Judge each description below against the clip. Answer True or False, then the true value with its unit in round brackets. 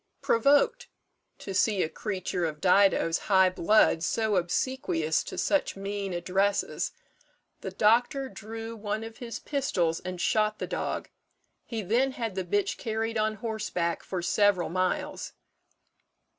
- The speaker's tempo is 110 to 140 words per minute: True (135 wpm)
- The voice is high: True (205 Hz)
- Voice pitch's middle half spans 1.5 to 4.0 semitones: True (3.6 semitones)